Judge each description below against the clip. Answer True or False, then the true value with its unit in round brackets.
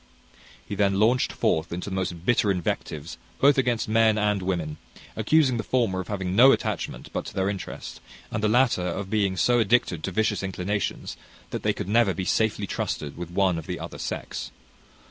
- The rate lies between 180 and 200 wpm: True (190 wpm)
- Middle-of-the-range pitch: False (100 Hz)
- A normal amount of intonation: True (3.5 semitones)